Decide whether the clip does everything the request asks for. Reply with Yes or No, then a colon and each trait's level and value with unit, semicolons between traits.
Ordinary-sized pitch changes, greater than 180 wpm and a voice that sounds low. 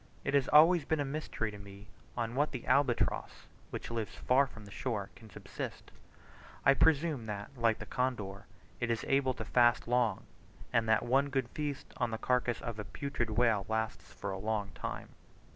Yes: average, 3.8 semitones; average, 190 wpm; low, 120 Hz